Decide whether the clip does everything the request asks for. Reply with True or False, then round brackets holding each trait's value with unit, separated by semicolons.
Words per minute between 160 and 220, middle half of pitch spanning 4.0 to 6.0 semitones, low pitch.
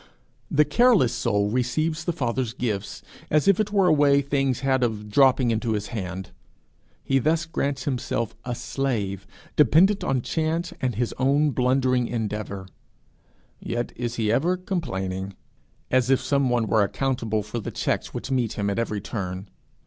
True (165 wpm; 4.6 semitones; 125 Hz)